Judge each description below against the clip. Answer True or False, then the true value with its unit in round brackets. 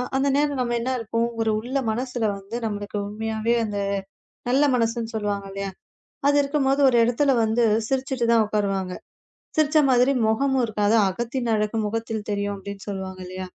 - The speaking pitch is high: True (225 Hz)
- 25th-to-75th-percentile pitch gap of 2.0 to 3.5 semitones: False (3.9 semitones)